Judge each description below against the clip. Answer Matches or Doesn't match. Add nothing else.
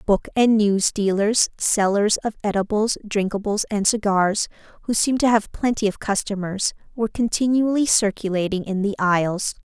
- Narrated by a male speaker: Doesn't match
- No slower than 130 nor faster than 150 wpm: Matches